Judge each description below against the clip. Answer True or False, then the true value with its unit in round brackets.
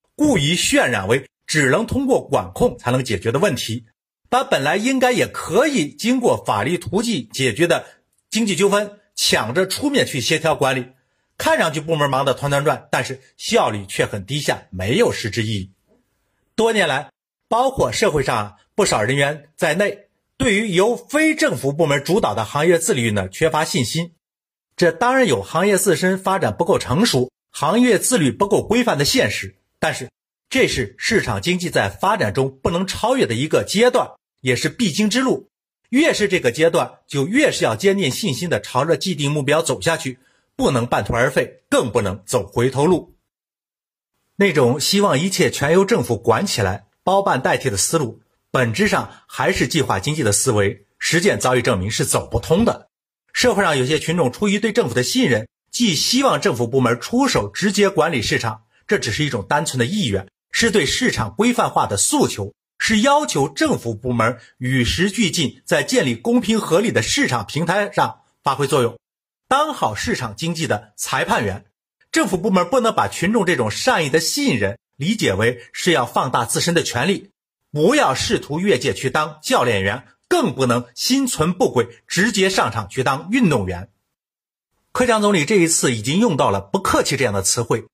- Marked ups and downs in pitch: True (8.8 semitones)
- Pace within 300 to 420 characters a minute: False (275 characters per minute)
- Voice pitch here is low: False (160 Hz)